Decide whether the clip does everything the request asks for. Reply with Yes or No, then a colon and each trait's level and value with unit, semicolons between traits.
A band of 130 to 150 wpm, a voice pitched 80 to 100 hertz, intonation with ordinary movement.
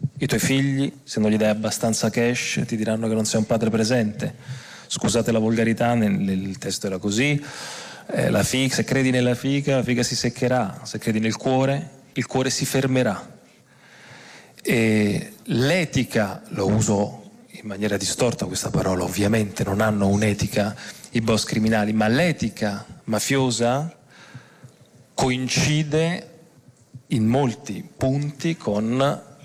No: slow, 135 wpm; low, 120 Hz; average, 3.9 semitones